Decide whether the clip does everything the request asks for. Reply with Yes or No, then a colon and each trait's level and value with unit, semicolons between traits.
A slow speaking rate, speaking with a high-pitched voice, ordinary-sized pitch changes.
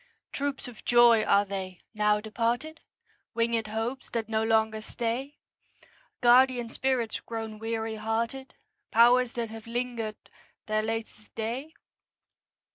No: slow, 120 wpm; high, 230 Hz; narrow, 1.8 semitones